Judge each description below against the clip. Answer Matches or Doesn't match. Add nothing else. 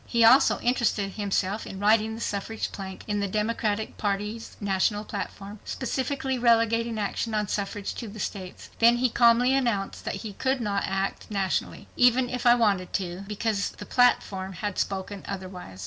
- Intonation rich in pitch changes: Doesn't match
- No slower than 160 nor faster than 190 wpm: Matches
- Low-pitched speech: Doesn't match